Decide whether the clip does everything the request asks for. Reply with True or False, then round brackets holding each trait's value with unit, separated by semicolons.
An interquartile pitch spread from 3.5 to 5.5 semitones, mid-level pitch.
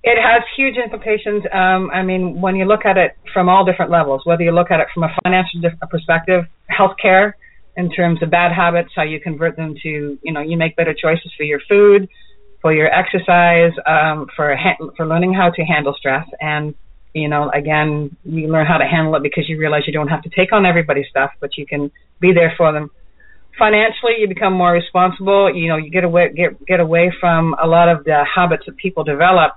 False (2.9 semitones; 170 Hz)